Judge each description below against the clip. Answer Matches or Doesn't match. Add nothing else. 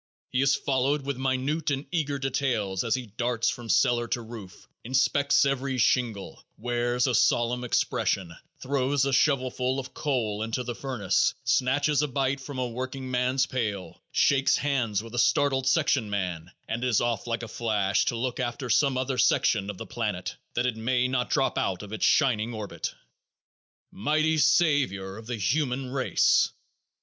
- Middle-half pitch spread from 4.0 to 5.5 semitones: Doesn't match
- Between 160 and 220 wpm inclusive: Matches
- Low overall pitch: Matches